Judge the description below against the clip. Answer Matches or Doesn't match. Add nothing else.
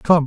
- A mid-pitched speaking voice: Matches